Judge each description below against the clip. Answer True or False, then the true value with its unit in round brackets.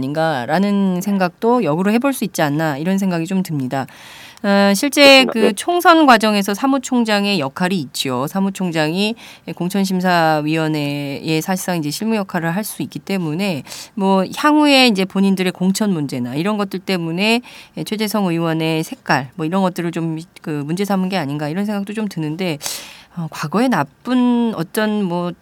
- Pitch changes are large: False (4.7 semitones)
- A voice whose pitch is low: False (185 Hz)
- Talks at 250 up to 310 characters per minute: False (330 characters per minute)